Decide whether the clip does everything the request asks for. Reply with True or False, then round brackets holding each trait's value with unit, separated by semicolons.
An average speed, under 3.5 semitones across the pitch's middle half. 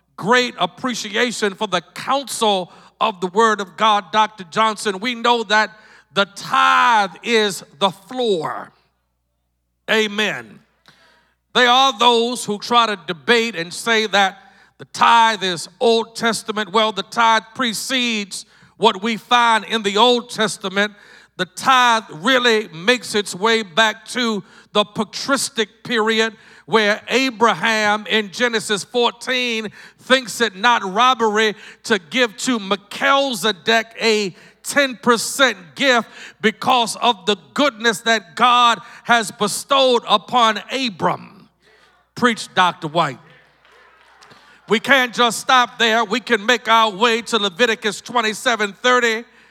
False (120 wpm; 2.8 semitones)